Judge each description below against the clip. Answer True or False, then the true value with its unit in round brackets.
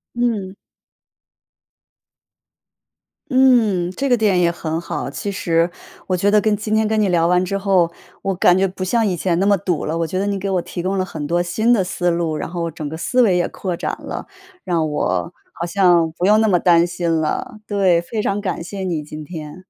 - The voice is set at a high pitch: False (180 Hz)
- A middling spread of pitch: True (3.0 semitones)